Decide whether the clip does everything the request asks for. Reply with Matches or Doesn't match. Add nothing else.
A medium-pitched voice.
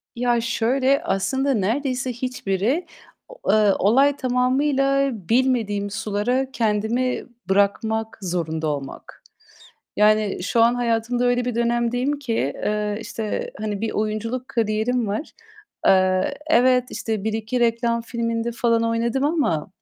Doesn't match